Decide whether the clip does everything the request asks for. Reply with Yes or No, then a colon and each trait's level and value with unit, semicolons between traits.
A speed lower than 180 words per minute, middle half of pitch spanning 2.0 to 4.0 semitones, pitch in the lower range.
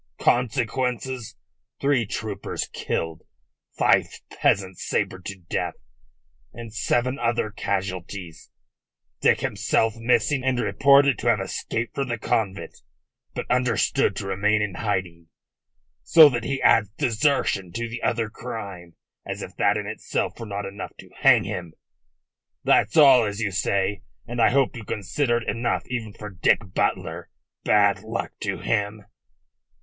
Yes: average, 140 wpm; average, 3.6 semitones; low, 110 Hz